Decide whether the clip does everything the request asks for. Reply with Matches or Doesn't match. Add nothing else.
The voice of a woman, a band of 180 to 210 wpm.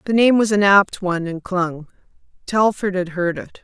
Matches